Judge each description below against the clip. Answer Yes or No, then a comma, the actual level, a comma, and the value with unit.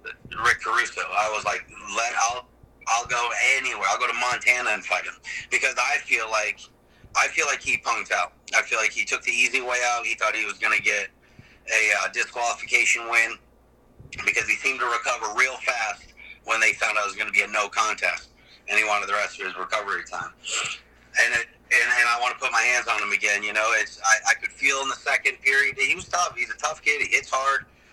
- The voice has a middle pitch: No, low, 120 Hz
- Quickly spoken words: Yes, fast, 230 wpm